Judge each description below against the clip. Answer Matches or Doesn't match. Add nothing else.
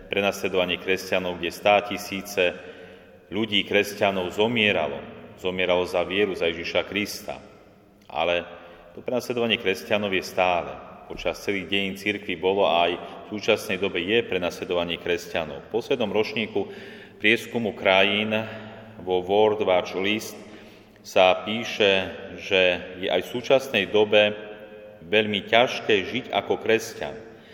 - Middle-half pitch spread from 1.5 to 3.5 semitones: Matches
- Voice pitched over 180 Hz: Doesn't match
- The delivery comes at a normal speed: Matches